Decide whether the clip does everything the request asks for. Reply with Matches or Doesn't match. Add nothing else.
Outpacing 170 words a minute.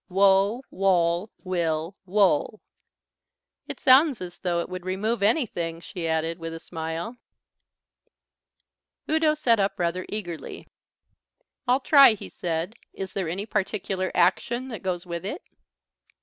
Doesn't match